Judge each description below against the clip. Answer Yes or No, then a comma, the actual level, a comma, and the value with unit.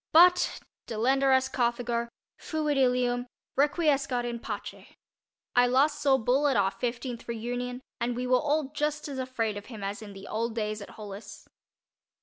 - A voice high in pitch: Yes, high, 245 Hz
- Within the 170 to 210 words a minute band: No, average, 150 wpm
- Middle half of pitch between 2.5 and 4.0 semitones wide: Yes, average, 2.9 semitones